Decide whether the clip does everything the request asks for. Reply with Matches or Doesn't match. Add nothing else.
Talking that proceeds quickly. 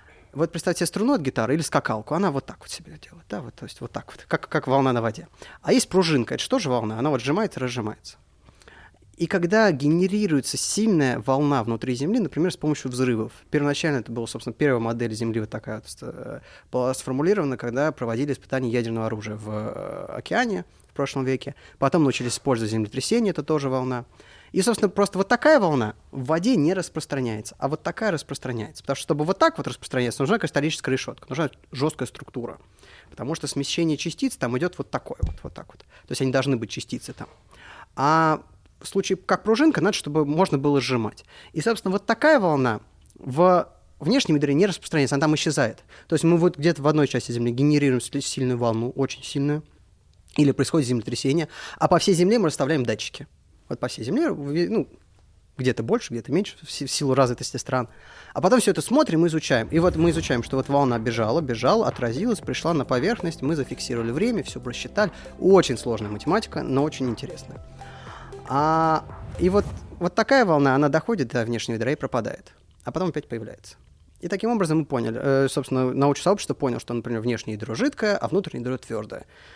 Matches